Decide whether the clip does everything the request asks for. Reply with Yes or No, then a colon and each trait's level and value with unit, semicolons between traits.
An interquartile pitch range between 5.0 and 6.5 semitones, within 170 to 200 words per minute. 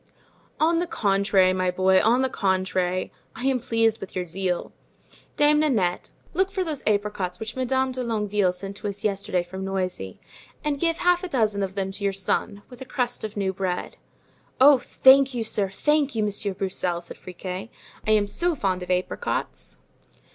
Yes: wide, 5.5 semitones; average, 185 wpm